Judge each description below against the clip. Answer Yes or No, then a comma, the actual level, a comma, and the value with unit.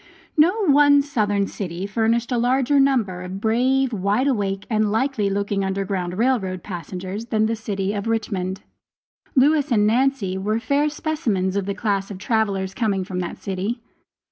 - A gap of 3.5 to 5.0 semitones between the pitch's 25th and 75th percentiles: Yes, average, 4.7 semitones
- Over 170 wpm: No, average, 165 wpm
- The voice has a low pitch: No, high, 215 Hz